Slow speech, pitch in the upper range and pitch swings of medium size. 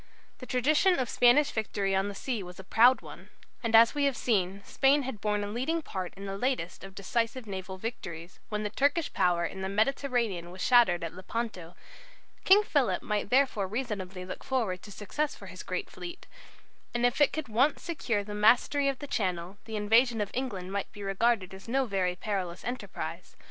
No: average, 195 wpm; high, 215 Hz; average, 5.0 semitones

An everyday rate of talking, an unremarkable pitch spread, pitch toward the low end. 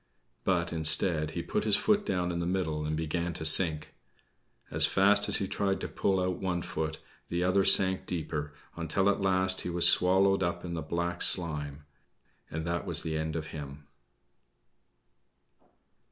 Yes: average, 170 wpm; average, 3.0 semitones; very low, 85 Hz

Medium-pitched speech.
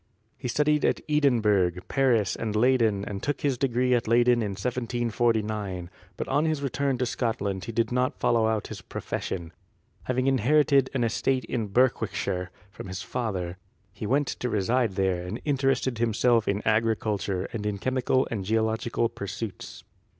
No: low, 115 Hz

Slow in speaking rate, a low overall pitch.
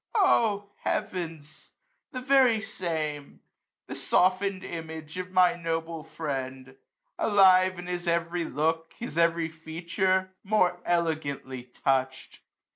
No: slow, 110 wpm; medium, 170 Hz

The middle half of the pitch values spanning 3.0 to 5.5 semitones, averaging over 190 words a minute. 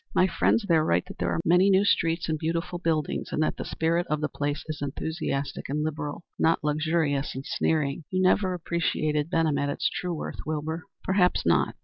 No: narrow, 2.5 semitones; average, 200 wpm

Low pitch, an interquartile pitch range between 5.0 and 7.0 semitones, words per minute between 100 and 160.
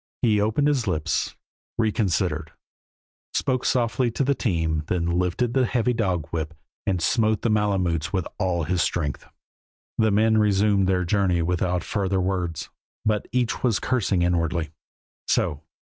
No: very low, 95 Hz; average, 4.3 semitones; average, 145 wpm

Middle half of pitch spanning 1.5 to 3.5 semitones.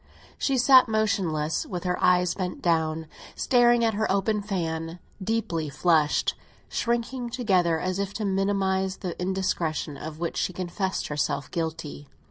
No: average, 4.6 semitones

